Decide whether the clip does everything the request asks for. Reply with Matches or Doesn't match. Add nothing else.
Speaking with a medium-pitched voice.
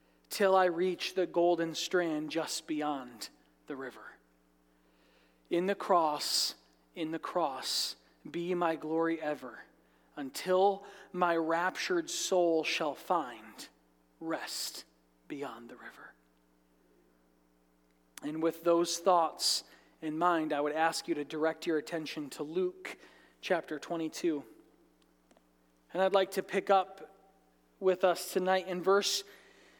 Matches